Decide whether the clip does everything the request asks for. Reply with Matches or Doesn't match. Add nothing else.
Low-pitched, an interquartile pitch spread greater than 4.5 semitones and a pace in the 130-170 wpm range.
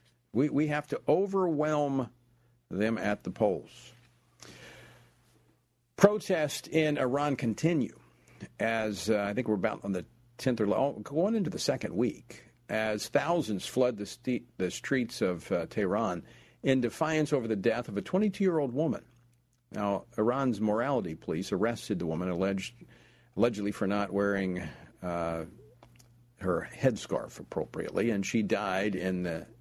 Matches